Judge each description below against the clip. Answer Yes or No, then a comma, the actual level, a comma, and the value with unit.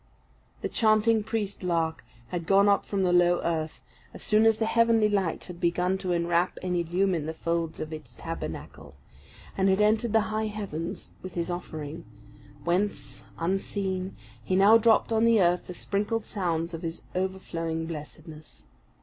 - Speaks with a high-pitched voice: No, medium, 180 Hz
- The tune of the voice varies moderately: Yes, average, 3.8 semitones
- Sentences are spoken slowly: No, average, 165 wpm